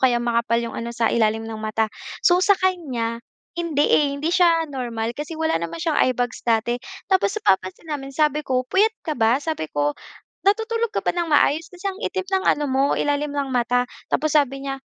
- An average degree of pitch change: No, wide, 5.9 semitones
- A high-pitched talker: Yes, very high, 275 Hz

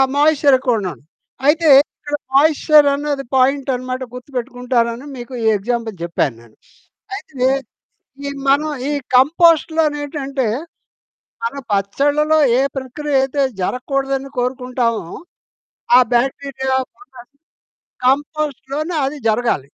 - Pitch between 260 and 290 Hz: Yes, very high, 270 Hz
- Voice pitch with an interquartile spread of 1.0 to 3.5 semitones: Yes, average, 2.9 semitones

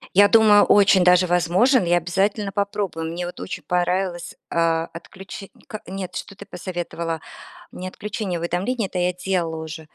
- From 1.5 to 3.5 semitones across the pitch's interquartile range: Yes, narrow, 2.5 semitones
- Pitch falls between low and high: Yes, medium, 180 Hz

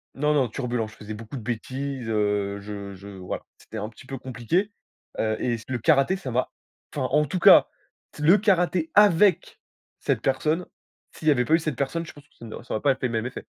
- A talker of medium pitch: No, low, 130 Hz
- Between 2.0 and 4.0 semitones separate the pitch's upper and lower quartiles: No, wide, 5.6 semitones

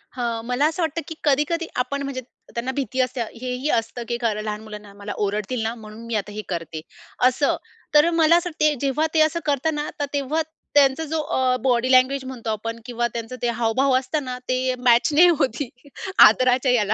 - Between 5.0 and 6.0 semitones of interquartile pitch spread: No, average, 4.0 semitones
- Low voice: No, very high, 255 Hz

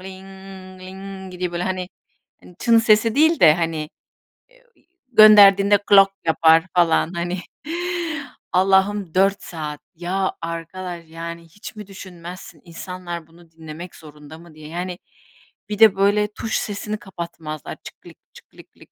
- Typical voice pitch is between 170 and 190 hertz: Yes, medium, 185 Hz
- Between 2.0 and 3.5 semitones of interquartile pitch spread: Yes, average, 2.8 semitones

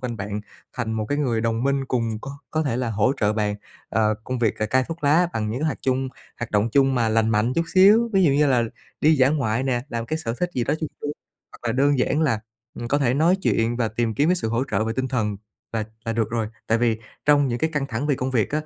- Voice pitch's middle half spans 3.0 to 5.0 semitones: Yes, average, 4.3 semitones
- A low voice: Yes, low, 125 Hz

